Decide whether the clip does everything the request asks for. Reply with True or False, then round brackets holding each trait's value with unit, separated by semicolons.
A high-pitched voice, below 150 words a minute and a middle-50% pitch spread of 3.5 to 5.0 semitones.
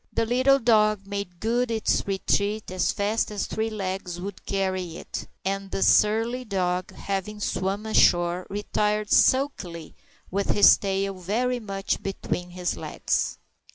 False (200 Hz; 140 wpm; 2.6 semitones)